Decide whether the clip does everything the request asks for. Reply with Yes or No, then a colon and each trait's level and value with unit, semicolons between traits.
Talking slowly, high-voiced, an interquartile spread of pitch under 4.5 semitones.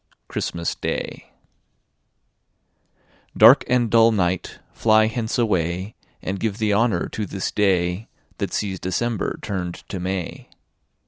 No: slow, 120 wpm; low, 100 Hz; average, 3.4 semitones